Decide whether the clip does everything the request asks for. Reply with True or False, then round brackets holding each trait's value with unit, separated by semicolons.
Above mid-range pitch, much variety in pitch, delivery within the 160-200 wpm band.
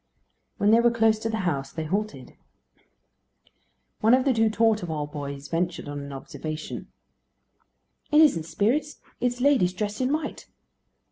False (210 Hz; 7.1 semitones; 150 wpm)